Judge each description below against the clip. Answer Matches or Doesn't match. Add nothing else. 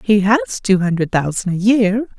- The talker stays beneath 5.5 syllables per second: Matches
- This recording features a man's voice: Doesn't match